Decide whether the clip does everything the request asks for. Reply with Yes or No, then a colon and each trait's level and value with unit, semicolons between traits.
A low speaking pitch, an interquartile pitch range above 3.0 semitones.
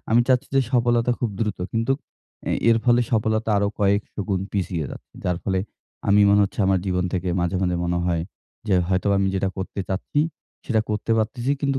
Yes: low, 100 Hz; average, 3.7 semitones